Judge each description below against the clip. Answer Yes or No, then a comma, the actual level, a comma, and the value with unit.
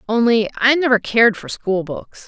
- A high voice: Yes, high, 225 Hz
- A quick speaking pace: No, average, 160 wpm